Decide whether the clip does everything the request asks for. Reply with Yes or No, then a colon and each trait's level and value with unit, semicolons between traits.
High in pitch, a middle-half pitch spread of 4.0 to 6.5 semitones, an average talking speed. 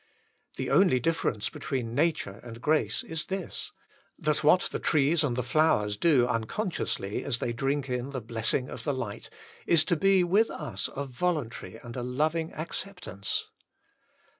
No: medium, 140 Hz; wide, 5.5 semitones; average, 160 wpm